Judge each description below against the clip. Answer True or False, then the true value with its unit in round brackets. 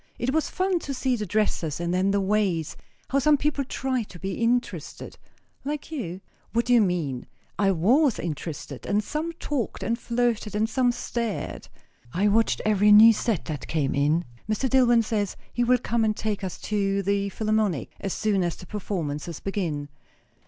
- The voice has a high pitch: True (210 Hz)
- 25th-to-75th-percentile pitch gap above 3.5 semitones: True (4.8 semitones)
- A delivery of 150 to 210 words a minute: True (180 wpm)